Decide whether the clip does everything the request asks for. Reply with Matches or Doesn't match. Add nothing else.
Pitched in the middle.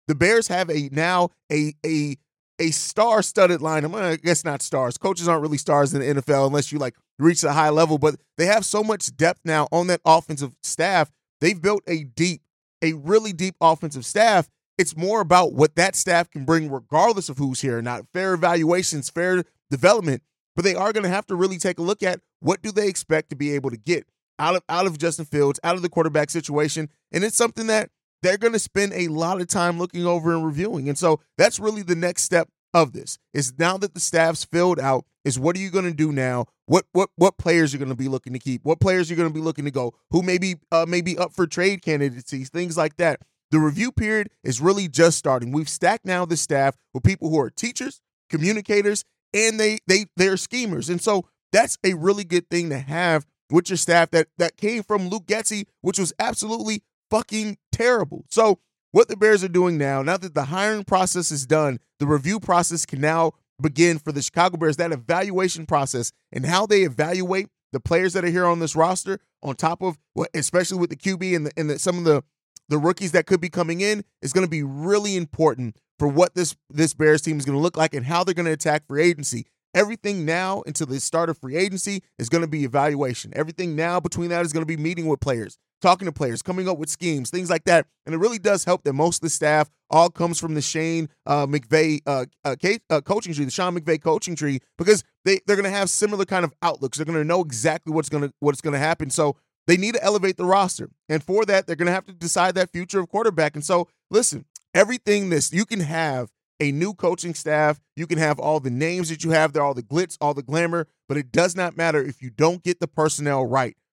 Matches